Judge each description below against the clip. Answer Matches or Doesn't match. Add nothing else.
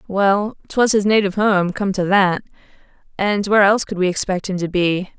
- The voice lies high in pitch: Matches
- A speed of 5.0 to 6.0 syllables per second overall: Matches